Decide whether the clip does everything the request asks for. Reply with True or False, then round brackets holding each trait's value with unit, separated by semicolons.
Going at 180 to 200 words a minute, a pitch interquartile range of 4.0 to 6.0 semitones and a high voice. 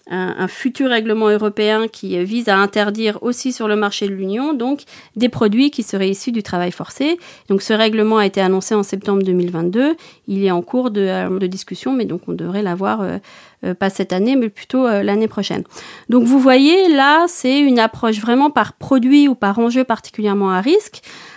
True (195 wpm; 4.5 semitones; 215 Hz)